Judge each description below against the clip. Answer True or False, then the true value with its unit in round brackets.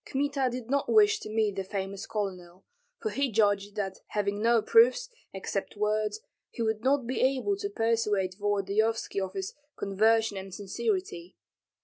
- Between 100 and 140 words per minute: False (155 wpm)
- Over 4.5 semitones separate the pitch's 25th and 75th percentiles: True (5.2 semitones)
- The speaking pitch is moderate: False (215 Hz)